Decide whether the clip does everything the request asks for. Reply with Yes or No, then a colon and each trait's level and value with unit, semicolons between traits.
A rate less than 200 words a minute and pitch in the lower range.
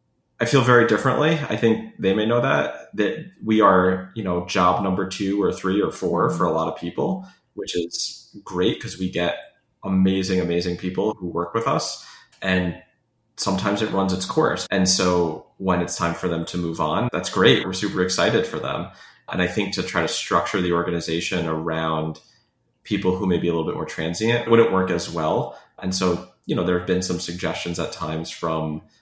No: fast, 205 wpm; very low, 90 Hz